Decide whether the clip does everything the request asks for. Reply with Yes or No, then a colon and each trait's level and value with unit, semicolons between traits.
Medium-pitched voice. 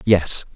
No: very low, 90 Hz